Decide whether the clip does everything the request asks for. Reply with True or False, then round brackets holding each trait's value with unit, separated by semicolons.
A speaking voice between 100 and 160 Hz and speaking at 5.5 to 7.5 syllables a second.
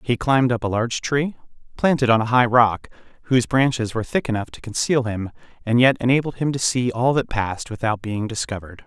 True (120 Hz; 6.0 syllables/s)